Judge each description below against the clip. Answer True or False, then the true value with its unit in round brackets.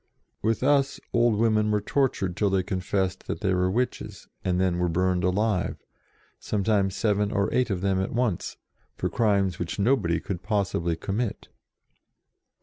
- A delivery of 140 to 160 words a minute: True (155 wpm)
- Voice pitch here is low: True (100 Hz)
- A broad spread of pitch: False (3.1 semitones)